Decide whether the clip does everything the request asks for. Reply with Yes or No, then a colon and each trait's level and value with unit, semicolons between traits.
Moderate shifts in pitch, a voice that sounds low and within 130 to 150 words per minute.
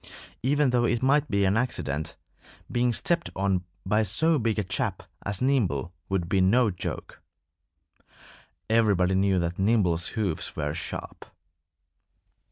Yes: average, 4.8 semitones; low, 100 Hz; slow, 135 wpm